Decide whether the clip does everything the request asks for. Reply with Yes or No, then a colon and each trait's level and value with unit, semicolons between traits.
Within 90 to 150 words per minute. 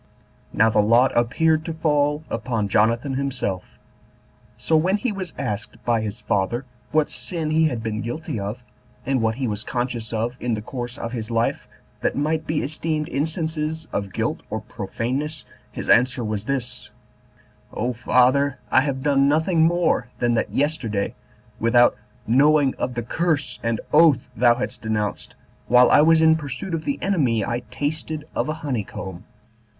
No: average, 165 wpm